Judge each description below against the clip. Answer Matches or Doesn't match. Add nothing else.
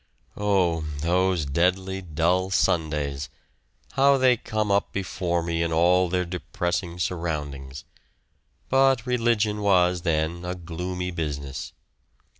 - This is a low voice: Matches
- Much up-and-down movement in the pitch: Doesn't match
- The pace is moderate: Doesn't match